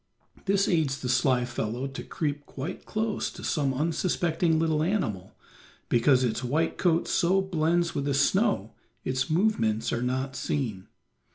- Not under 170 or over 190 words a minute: No, average, 150 wpm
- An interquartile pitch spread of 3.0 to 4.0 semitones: No, average, 5.2 semitones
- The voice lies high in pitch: No, medium, 145 Hz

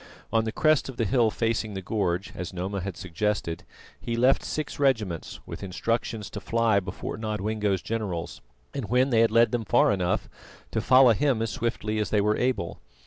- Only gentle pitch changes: No, average, 3.0 semitones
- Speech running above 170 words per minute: Yes, average, 190 wpm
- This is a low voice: Yes, low, 110 Hz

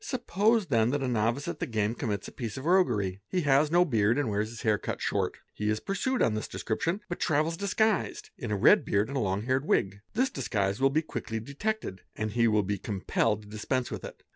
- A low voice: Yes, low, 120 Hz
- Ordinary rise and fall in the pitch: No, wide, 6.8 semitones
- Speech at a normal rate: No, fast, 240 wpm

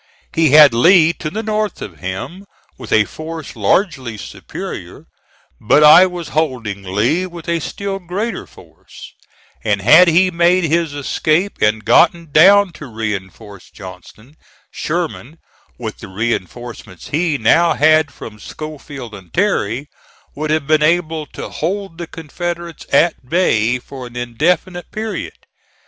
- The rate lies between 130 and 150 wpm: Yes, average, 140 wpm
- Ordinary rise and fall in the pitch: No, wide, 6.8 semitones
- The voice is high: No, medium, 155 Hz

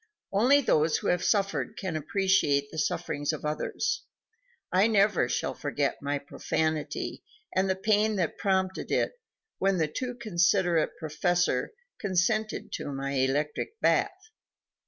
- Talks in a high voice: No, medium, 180 Hz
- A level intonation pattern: No, average, 5.1 semitones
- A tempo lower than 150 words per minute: Yes, slow, 135 wpm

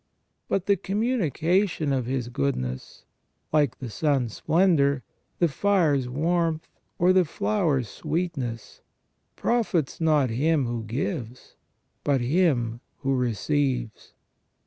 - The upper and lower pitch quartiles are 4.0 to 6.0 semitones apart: Yes, wide, 5.5 semitones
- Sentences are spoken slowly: Yes, slow, 110 wpm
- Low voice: No, medium, 145 Hz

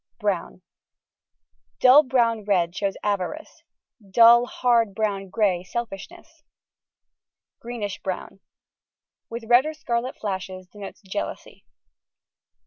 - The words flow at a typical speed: No, slow, 95 wpm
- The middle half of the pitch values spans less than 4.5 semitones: Yes, average, 3.6 semitones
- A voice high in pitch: Yes, high, 215 Hz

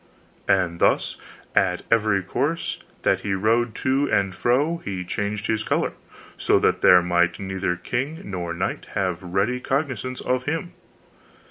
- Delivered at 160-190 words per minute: No, average, 145 wpm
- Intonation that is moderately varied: No, wide, 5.8 semitones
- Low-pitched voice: Yes, low, 105 Hz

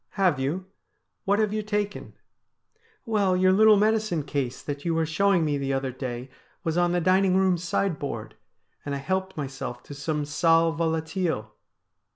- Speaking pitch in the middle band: Yes, medium, 165 Hz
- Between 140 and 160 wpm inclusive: No, average, 180 wpm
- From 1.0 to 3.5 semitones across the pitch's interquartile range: No, average, 5.1 semitones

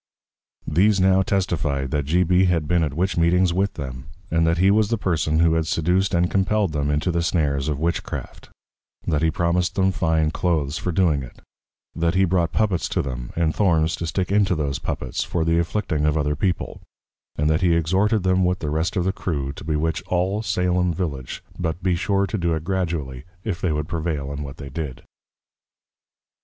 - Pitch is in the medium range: No, very low, 85 Hz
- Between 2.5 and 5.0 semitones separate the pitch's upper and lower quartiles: Yes, average, 3.4 semitones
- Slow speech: No, average, 200 wpm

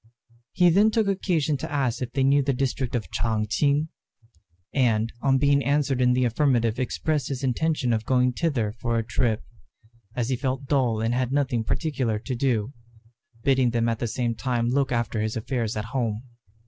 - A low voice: Yes, low, 125 Hz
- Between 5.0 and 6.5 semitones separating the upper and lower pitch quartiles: No, average, 3.3 semitones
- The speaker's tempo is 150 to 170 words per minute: No, average, 185 wpm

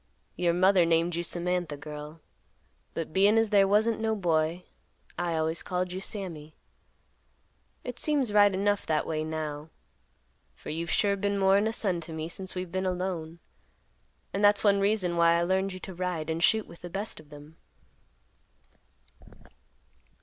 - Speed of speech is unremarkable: Yes, average, 165 wpm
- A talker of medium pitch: Yes, medium, 180 Hz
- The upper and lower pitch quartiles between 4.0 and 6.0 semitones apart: No, average, 3.5 semitones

